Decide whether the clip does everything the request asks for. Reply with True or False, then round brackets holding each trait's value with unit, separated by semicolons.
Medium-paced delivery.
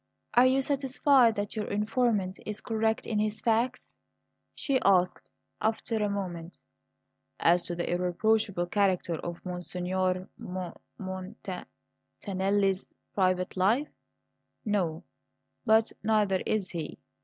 False (120 wpm)